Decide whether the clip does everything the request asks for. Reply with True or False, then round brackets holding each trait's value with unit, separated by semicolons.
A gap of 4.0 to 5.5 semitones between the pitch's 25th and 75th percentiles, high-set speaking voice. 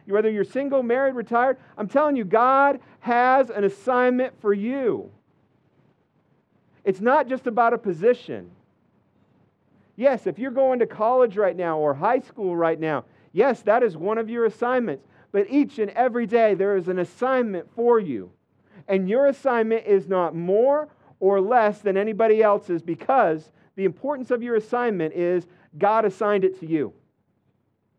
True (4.6 semitones; 220 Hz)